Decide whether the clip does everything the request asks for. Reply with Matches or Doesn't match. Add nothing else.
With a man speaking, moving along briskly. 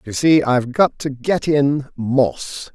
Doesn't match